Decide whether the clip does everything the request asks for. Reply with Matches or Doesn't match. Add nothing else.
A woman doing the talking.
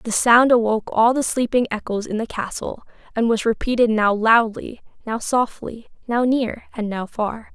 Matches